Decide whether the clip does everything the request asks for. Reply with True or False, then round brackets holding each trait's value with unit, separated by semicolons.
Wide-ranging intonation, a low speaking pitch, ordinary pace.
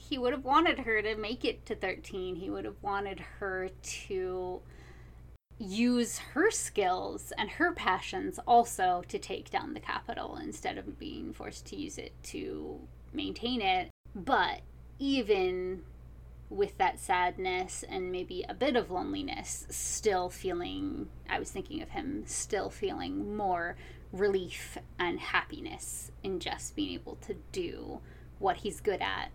False (8.3 semitones; 200 Hz; 145 wpm)